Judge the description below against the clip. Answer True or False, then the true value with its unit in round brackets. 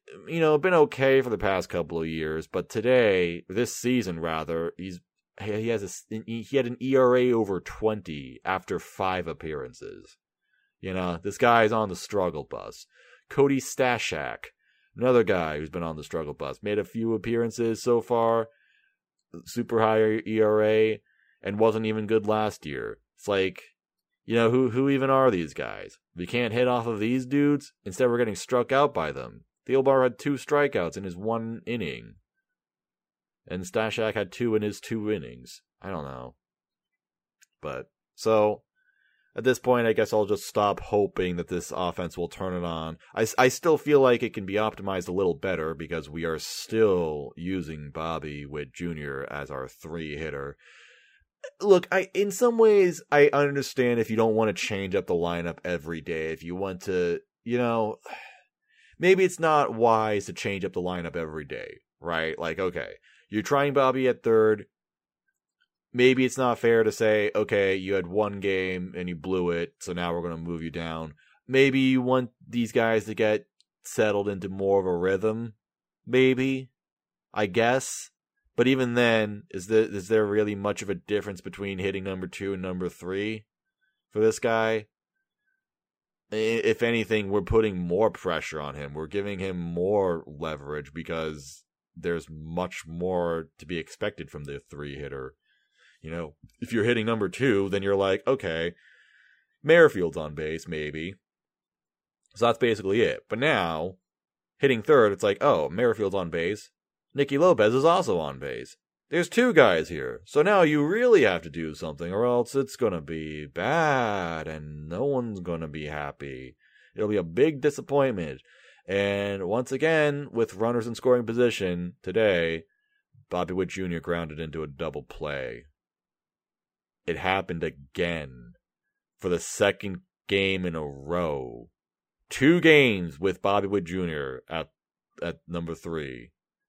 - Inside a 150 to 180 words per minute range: True (165 wpm)